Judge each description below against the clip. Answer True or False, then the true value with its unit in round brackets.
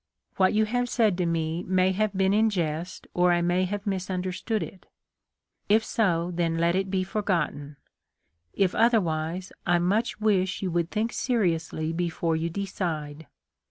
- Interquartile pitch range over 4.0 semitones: False (3.3 semitones)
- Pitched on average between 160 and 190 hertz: True (185 Hz)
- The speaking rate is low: False (165 wpm)